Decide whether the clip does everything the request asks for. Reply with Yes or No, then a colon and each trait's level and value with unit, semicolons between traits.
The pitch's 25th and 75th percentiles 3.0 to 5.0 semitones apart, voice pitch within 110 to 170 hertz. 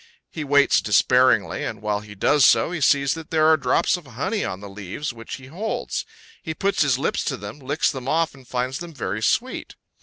No: wide, 5.5 semitones; medium, 140 Hz